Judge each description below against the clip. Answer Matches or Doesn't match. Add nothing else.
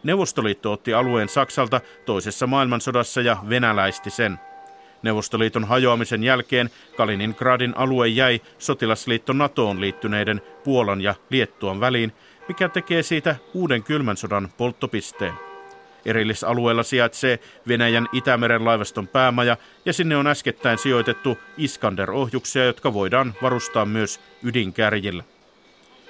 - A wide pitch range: Doesn't match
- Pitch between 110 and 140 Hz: Matches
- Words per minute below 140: Matches